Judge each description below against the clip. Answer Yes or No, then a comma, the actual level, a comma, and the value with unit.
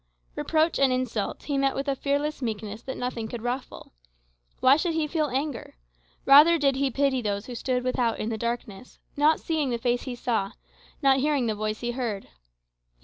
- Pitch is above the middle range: Yes, very high, 255 Hz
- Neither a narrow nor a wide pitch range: Yes, average, 3.3 semitones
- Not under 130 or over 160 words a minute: No, average, 190 wpm